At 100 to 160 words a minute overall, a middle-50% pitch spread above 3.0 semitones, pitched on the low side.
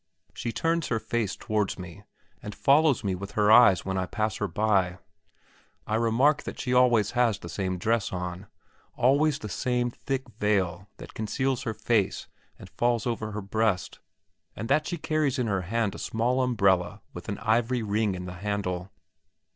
No: average, 180 wpm; average, 4.1 semitones; low, 110 Hz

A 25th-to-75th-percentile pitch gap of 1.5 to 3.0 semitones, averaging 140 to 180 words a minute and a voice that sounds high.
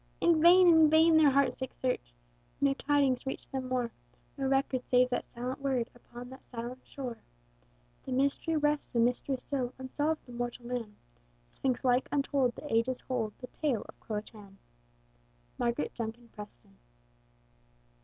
Yes: narrow, 2.6 semitones; average, 160 wpm; very high, 255 Hz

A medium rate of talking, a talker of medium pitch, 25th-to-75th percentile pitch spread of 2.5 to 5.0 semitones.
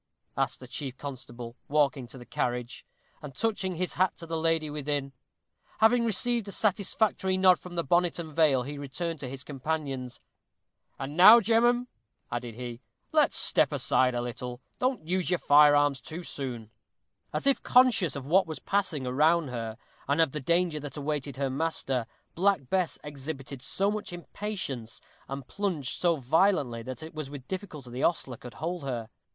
No: average, 175 wpm; medium, 150 Hz; wide, 5.5 semitones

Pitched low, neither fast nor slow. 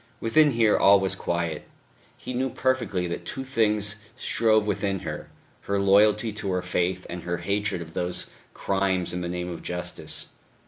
Yes: low, 100 Hz; average, 170 wpm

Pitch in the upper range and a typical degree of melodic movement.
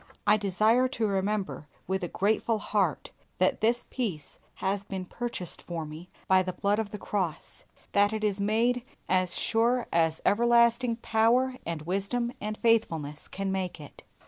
Yes: high, 205 Hz; average, 3.8 semitones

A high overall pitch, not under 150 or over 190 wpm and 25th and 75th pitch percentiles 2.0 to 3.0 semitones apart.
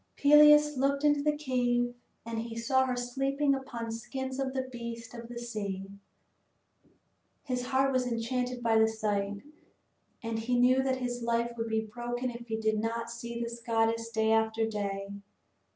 Yes: high, 235 Hz; average, 170 wpm; narrow, 2.5 semitones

